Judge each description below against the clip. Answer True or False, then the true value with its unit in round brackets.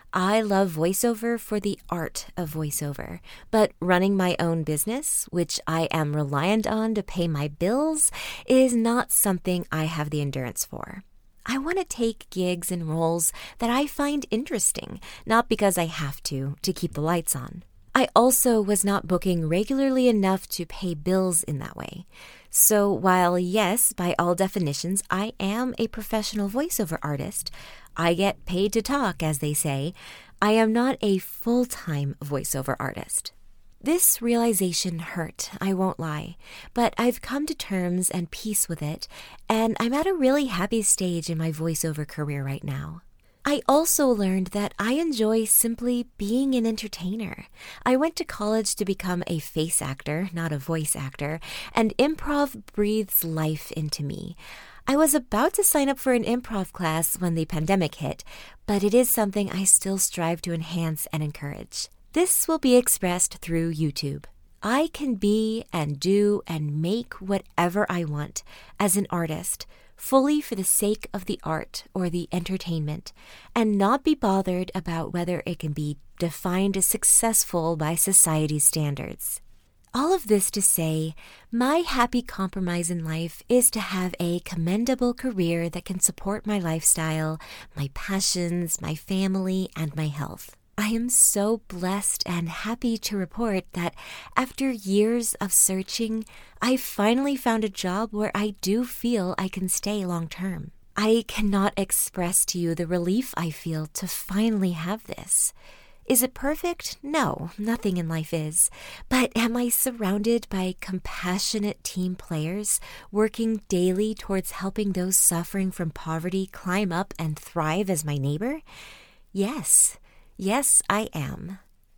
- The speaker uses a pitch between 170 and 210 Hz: True (190 Hz)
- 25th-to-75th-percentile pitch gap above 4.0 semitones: True (5.2 semitones)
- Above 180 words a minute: False (160 wpm)